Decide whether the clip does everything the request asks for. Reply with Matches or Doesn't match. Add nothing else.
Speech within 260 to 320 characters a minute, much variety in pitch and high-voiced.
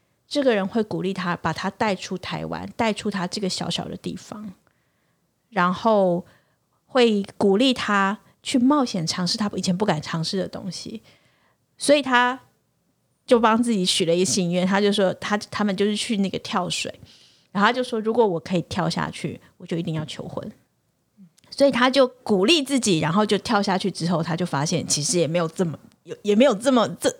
Doesn't match